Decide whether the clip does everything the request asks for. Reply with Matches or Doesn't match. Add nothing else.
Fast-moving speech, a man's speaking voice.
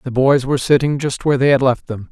Matches